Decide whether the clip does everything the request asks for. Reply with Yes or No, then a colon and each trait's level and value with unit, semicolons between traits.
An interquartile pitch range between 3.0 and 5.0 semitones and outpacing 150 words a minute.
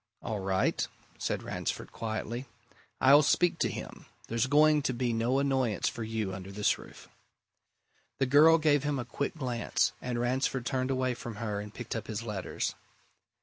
Yes: average, 3.6 semitones; average, 170 wpm